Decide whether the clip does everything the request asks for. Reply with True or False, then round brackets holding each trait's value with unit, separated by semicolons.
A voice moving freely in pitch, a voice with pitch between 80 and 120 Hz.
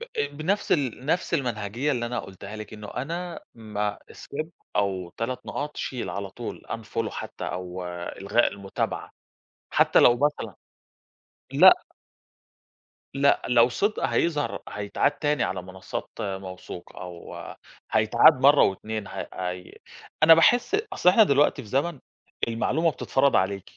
True (6.6 semitones; 115 Hz)